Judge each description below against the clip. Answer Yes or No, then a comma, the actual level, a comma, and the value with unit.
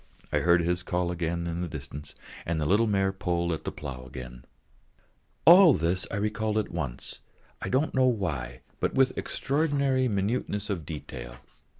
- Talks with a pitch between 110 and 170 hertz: No, very low, 90 Hz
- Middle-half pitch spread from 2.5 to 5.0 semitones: No, wide, 5.5 semitones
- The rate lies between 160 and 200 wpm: Yes, average, 175 wpm